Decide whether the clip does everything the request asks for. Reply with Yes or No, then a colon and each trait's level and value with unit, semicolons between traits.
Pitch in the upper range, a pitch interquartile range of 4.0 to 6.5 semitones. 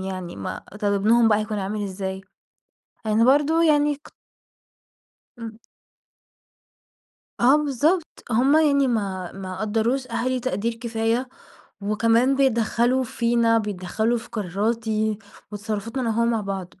No: high, 225 Hz; average, 3.5 semitones